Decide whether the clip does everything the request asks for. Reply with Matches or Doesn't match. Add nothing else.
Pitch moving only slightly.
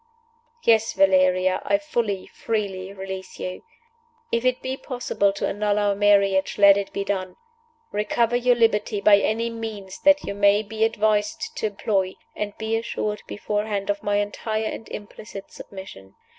Matches